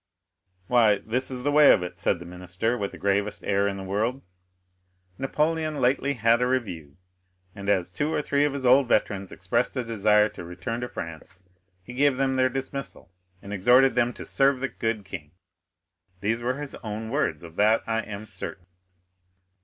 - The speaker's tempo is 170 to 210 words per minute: Yes, average, 185 wpm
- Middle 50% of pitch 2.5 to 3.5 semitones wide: No, average, 4.8 semitones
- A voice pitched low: Yes, low, 115 Hz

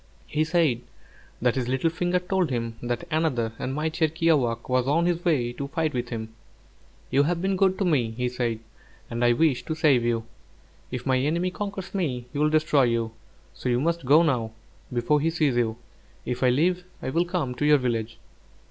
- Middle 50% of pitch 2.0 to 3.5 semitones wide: No, average, 5.3 semitones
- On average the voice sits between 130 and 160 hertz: Yes, medium, 140 Hz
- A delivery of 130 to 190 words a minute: No, average, 200 wpm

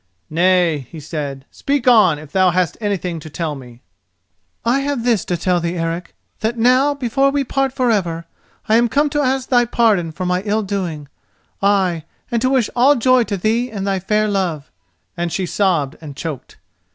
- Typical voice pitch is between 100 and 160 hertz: No, high, 195 Hz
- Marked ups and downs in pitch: Yes, wide, 6.3 semitones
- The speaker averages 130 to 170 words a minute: No, average, 190 wpm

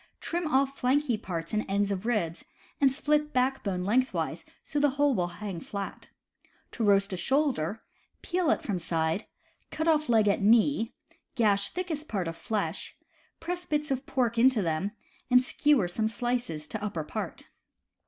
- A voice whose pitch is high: Yes, high, 230 Hz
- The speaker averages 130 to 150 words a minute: No, average, 165 wpm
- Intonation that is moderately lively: No, wide, 5.9 semitones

